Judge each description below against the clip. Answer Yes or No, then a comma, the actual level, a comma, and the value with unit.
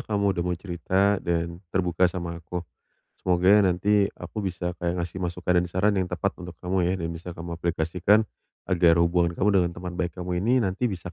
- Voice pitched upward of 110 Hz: No, very low, 90 Hz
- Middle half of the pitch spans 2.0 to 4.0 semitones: No, narrow, 1.6 semitones